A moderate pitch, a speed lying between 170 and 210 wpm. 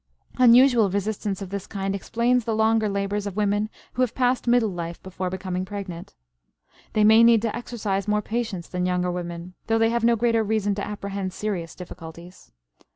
No: high, 205 Hz; average, 180 wpm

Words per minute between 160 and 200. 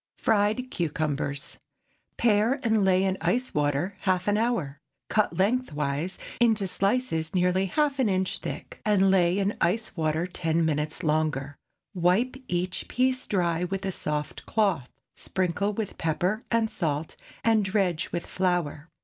No: average, 145 wpm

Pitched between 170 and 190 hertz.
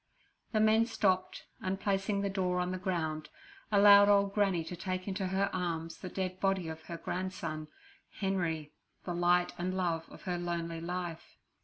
Yes: medium, 185 Hz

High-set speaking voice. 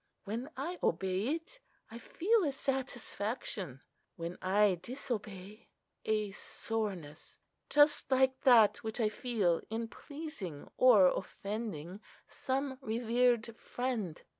Yes: high, 225 Hz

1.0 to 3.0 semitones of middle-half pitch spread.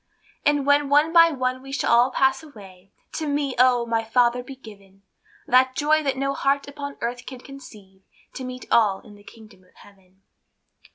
No: average, 4.4 semitones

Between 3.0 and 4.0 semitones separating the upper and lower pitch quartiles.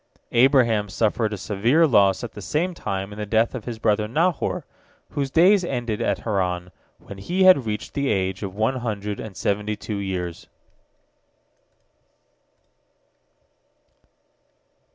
No: average, 4.6 semitones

